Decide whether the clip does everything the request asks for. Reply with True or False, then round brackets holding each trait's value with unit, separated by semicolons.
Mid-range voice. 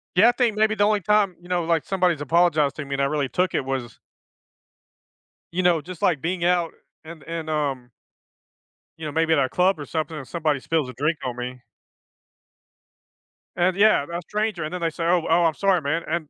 True (165 Hz)